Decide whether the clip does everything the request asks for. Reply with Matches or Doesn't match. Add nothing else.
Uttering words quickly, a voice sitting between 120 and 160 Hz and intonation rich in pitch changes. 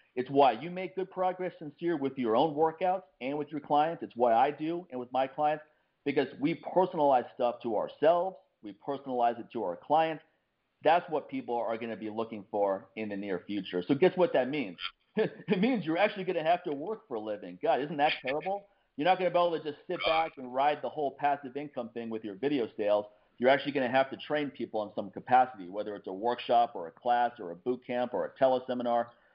Matches